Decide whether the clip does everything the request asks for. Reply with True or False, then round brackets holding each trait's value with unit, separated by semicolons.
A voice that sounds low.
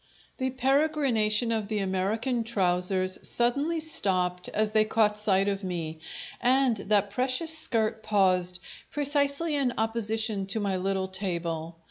False (215 Hz)